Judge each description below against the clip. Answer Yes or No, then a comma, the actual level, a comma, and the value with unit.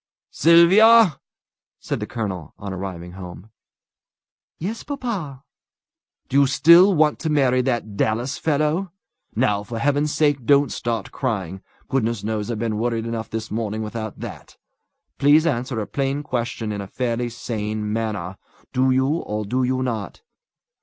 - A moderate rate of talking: Yes, average, 145 wpm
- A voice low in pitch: Yes, low, 120 Hz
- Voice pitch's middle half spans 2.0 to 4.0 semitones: No, average, 5.1 semitones